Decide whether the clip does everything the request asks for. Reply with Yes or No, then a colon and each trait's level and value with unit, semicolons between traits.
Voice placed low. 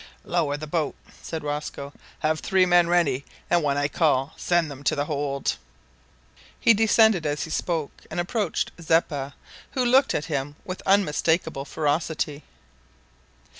No: medium, 155 Hz